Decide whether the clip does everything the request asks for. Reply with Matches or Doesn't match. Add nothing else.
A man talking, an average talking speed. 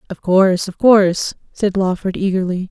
Doesn't match